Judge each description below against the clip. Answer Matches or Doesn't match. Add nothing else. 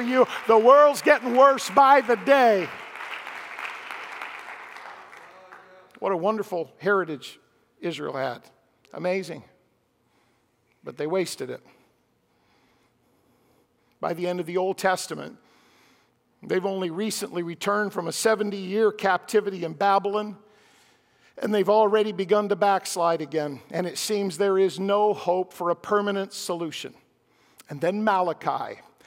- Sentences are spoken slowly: Matches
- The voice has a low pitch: Doesn't match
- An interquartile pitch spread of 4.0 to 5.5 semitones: Doesn't match